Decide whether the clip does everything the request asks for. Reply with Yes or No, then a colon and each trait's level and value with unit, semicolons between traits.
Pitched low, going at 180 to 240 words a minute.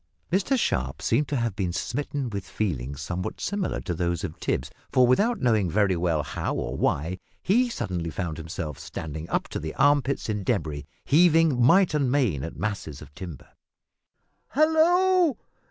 No: low, 105 Hz; average, 165 wpm